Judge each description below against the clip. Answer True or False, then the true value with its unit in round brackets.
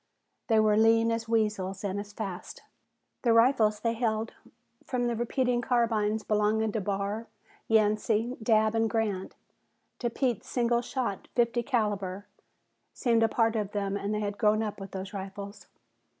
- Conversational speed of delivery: True (155 wpm)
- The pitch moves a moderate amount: False (2.0 semitones)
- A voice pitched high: True (220 Hz)